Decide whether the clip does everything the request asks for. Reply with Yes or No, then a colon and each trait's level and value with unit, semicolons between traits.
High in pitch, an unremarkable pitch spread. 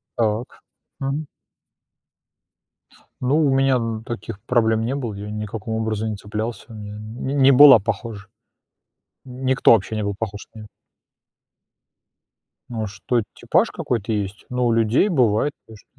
No: low, 115 Hz; average, 3.2 semitones